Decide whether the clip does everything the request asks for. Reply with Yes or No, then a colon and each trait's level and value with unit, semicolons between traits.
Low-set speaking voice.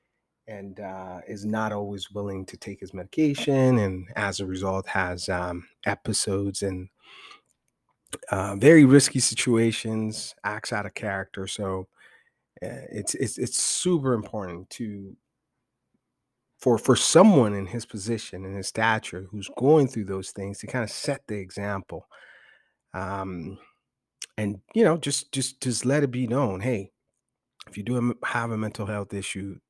Yes: low, 105 Hz